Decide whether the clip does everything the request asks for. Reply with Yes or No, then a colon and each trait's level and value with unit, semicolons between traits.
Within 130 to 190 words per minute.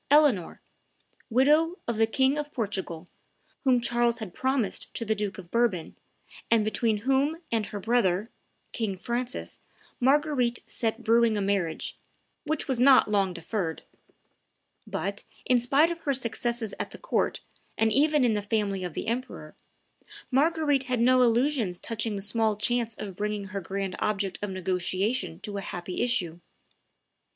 Yes: average, 155 wpm